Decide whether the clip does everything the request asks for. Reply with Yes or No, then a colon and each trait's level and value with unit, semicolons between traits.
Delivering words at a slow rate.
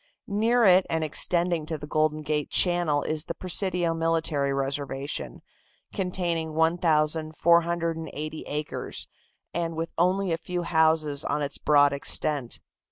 Yes: slow, 125 wpm